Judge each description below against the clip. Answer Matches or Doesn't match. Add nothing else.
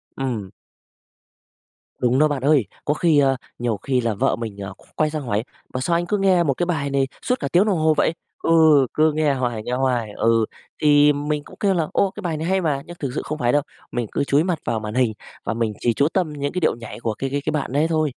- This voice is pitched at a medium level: Matches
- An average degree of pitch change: Matches